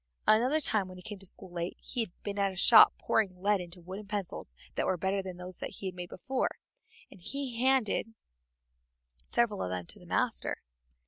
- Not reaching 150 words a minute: No, average, 200 wpm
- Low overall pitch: No, high, 195 Hz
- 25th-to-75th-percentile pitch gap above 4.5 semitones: No, average, 3.6 semitones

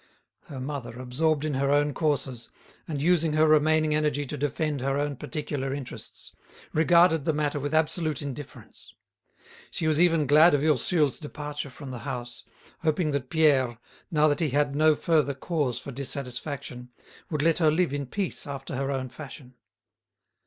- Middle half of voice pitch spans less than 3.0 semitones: Yes, narrow, 2.4 semitones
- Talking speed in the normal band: Yes, average, 165 wpm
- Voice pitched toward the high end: No, medium, 145 Hz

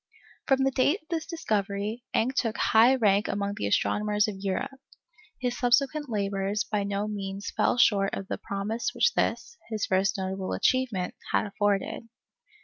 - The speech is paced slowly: No, average, 160 wpm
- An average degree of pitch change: Yes, average, 3.9 semitones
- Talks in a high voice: Yes, high, 210 Hz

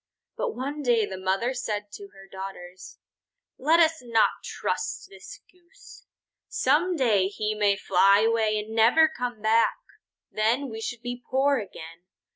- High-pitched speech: Yes, high, 230 Hz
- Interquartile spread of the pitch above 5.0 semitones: Yes, wide, 5.4 semitones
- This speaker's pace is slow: No, average, 150 wpm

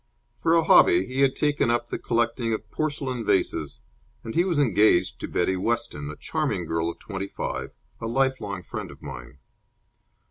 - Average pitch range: No, wide, 6.4 semitones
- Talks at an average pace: Yes, average, 175 wpm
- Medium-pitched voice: No, low, 115 Hz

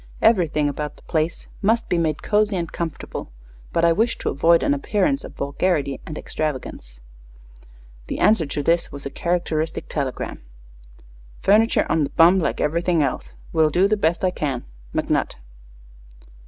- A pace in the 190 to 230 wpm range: No, average, 155 wpm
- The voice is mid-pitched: Yes, medium, 165 Hz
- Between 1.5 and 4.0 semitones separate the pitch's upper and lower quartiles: Yes, average, 3.7 semitones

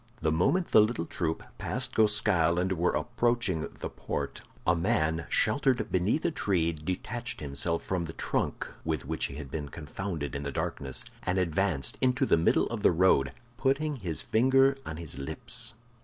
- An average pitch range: No, wide, 7.0 semitones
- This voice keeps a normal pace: Yes, average, 170 wpm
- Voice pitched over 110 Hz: No, very low, 90 Hz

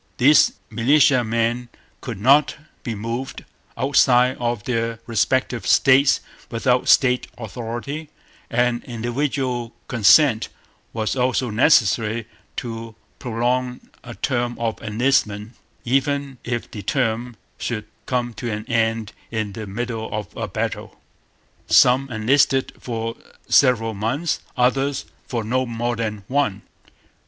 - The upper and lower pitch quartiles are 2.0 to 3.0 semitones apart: Yes, narrow, 2.4 semitones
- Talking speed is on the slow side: Yes, slow, 115 wpm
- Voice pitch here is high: No, low, 120 Hz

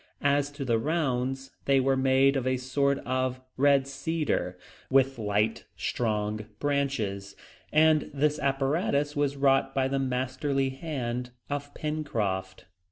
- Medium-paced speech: No, slow, 130 wpm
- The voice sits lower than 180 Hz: Yes, low, 135 Hz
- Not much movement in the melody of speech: Yes, narrow, 2.3 semitones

